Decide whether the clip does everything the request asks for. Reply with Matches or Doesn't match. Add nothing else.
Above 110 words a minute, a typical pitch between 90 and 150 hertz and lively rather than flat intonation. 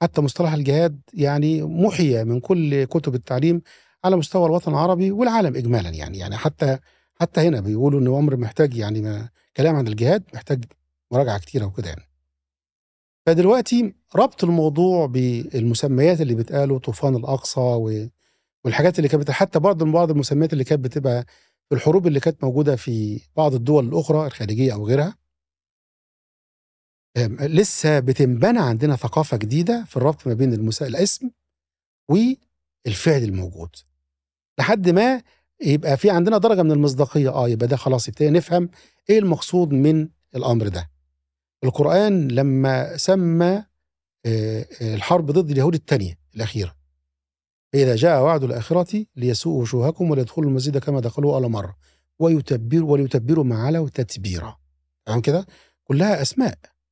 Matches